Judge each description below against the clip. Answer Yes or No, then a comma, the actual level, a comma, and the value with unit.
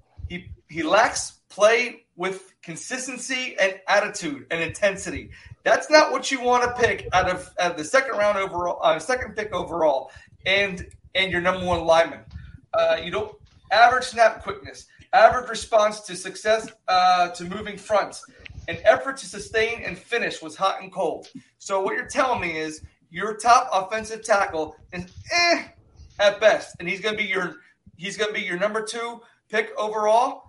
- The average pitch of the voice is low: No, high, 205 Hz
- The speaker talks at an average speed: Yes, average, 170 wpm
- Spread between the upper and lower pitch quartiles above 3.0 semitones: Yes, average, 4.4 semitones